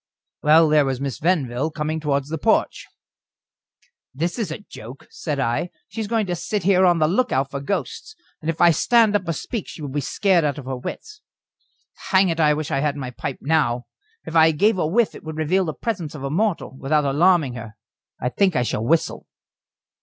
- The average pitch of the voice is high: No, medium, 155 Hz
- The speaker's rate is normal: No, fast, 215 wpm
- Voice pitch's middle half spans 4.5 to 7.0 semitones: Yes, average, 4.9 semitones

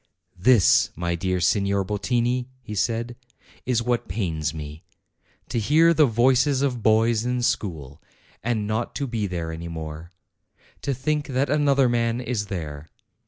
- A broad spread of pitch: Yes, wide, 5.9 semitones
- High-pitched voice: No, low, 115 Hz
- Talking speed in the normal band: Yes, average, 150 wpm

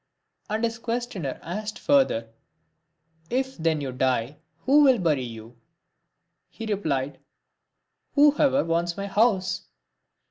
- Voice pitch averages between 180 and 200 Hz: Yes, medium, 185 Hz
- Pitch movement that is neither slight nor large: No, wide, 8.5 semitones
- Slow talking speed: Yes, slow, 130 wpm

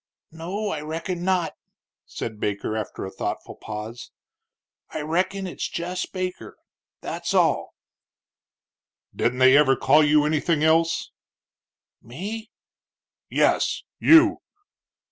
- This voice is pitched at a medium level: Yes, medium, 160 Hz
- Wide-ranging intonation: Yes, wide, 5.8 semitones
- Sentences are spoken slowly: Yes, slow, 105 wpm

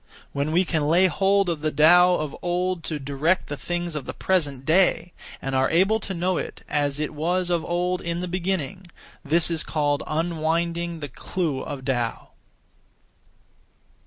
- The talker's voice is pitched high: No, medium, 170 Hz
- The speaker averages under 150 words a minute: No, average, 170 wpm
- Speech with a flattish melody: No, average, 3.2 semitones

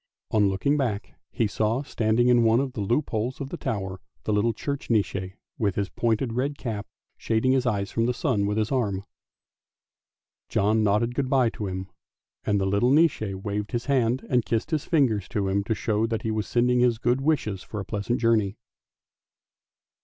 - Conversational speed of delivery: Yes, average, 195 wpm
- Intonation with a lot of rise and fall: No, average, 3.3 semitones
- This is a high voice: No, low, 110 Hz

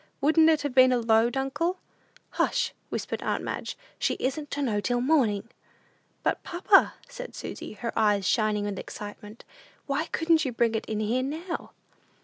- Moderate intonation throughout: No, wide, 6.1 semitones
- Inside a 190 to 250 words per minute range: No, average, 165 wpm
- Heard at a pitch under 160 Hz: No, very high, 255 Hz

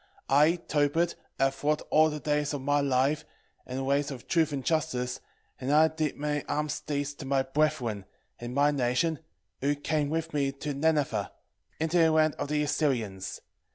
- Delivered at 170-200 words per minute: Yes, average, 180 wpm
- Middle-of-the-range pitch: Yes, medium, 145 Hz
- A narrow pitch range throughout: Yes, narrow, 2.2 semitones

